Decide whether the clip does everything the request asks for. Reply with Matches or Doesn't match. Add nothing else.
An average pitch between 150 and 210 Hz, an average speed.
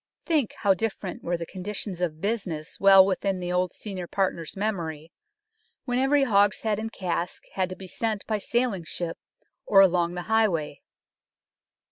Matches